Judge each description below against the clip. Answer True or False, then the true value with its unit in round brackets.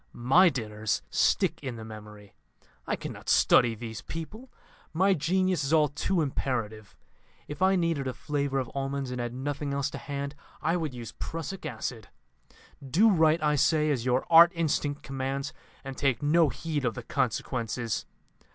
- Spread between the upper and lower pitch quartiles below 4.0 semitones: False (4.5 semitones)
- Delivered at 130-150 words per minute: False (165 wpm)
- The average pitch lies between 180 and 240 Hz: False (140 Hz)